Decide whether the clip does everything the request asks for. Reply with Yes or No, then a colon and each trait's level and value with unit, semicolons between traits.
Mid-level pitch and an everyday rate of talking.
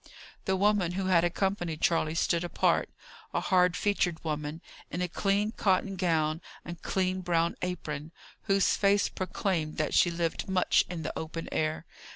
Yes: medium, 175 Hz; average, 160 wpm